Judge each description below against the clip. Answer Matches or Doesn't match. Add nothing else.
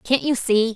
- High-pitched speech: Matches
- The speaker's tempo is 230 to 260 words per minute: Matches